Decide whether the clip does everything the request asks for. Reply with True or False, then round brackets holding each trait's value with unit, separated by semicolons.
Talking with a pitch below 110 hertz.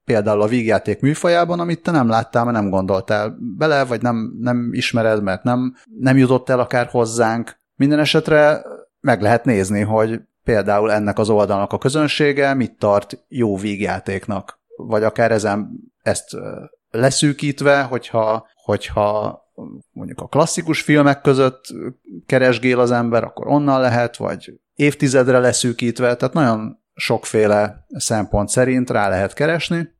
False (120 Hz)